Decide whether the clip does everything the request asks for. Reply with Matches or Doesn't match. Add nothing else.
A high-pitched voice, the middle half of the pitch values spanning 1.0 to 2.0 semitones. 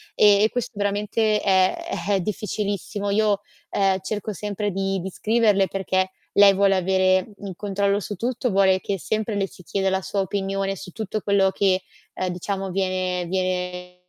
Matches